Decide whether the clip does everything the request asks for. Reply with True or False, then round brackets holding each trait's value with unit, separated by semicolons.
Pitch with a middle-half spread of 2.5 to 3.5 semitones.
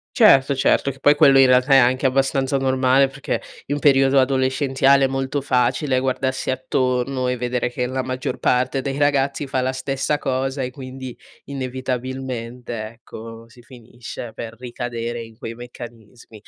False (1.5 semitones)